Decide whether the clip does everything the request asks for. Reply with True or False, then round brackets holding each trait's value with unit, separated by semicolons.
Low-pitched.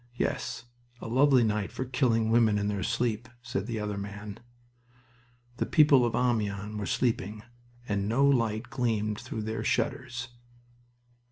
True (110 Hz)